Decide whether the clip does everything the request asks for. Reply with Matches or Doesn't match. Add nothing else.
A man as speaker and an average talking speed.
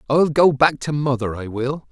Doesn't match